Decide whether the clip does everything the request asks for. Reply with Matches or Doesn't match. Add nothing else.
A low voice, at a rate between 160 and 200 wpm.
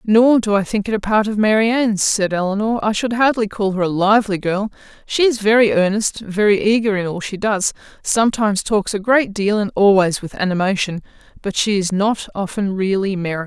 Doesn't match